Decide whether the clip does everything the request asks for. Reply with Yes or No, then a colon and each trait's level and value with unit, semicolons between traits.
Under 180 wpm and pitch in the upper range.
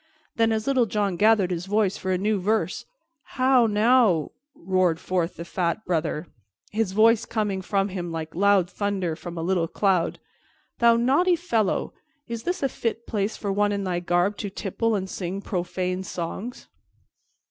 Yes: average, 170 wpm; high, 200 Hz